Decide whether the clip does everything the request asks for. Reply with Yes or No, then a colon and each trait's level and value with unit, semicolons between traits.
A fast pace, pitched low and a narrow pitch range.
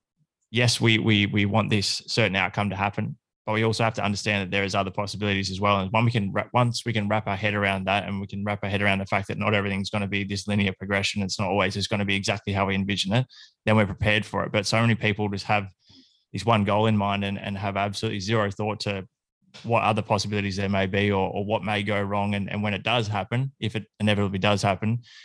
Yes: fast, 265 wpm; low, 105 Hz; narrow, 1.5 semitones